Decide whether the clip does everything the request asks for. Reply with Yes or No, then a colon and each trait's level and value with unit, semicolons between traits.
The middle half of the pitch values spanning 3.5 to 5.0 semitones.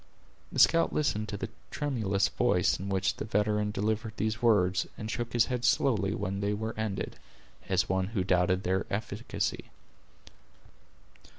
No: narrow, 2.6 semitones